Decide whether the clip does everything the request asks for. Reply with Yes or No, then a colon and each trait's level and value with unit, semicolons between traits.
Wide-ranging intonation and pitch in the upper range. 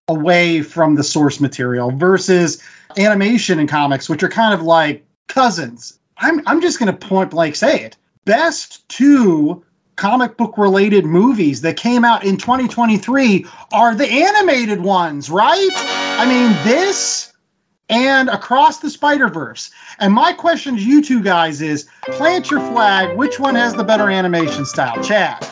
Yes: wide, 7.8 semitones; high, 205 Hz